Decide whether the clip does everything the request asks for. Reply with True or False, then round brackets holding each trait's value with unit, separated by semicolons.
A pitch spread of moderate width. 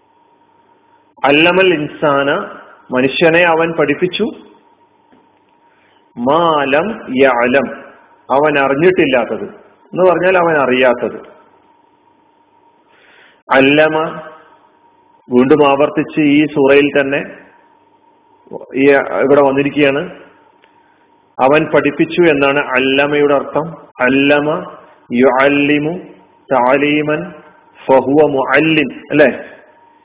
True (4.8 semitones)